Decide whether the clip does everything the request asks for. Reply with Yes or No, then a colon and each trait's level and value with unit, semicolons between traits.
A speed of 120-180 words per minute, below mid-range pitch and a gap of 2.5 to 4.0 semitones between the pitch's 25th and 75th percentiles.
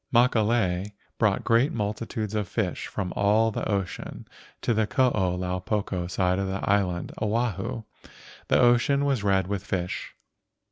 Yes: average, 150 wpm; low, 105 Hz; average, 3.5 semitones